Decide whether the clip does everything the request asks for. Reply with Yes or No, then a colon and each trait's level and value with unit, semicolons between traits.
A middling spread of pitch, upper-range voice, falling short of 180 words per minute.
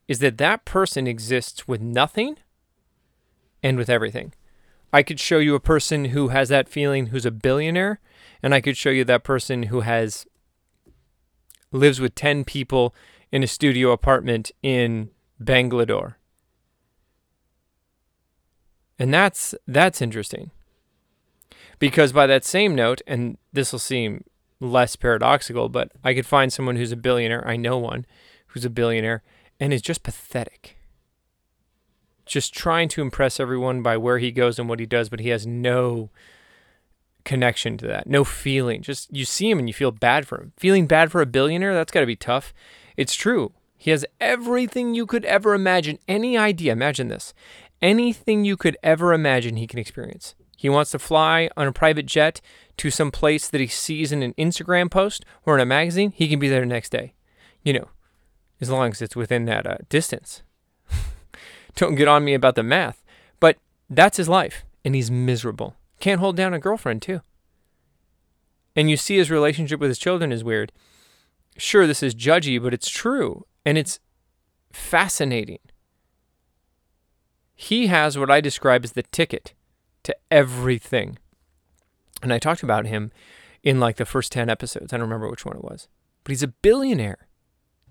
No: average, 4.8 semitones; low, 130 Hz; average, 170 wpm